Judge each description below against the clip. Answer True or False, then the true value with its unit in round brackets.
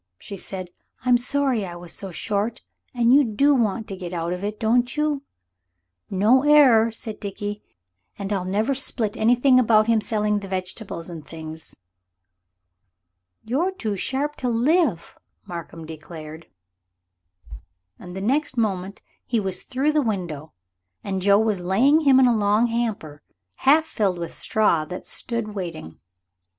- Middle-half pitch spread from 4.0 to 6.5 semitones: True (5.1 semitones)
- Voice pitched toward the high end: True (215 Hz)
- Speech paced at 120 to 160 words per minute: True (145 wpm)